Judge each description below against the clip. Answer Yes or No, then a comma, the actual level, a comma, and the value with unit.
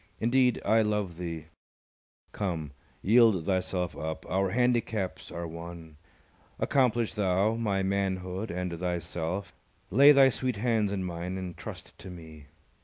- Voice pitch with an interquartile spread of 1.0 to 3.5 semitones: No, average, 4.3 semitones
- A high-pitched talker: No, very low, 95 Hz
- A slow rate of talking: Yes, slow, 130 wpm